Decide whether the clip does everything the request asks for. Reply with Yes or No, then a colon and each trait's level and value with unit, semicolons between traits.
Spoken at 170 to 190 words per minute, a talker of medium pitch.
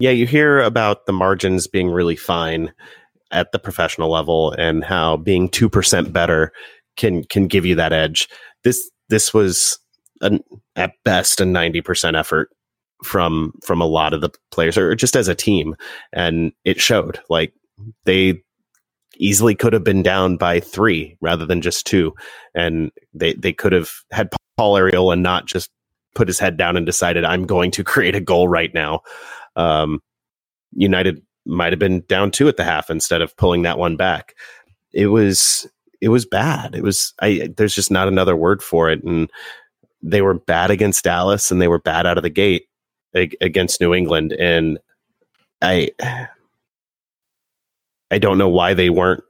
No: average, 175 wpm; very low, 90 Hz